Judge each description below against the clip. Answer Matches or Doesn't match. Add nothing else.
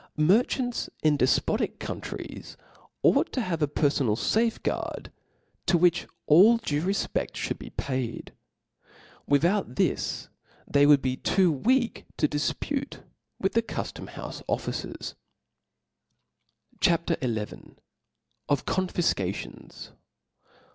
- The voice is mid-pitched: Matches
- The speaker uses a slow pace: Matches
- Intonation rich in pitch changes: Matches